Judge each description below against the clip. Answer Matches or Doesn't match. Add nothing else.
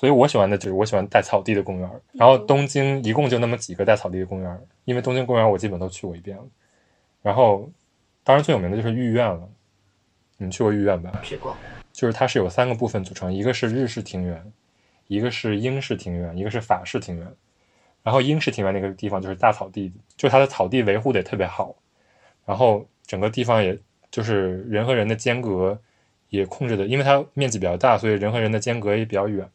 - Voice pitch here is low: Matches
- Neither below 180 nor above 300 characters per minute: Doesn't match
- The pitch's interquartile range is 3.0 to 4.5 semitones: Matches